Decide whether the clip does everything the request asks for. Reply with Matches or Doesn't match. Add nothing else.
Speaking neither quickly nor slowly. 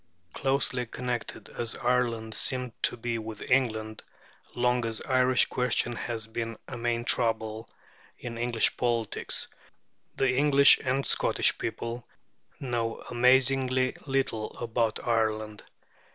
Doesn't match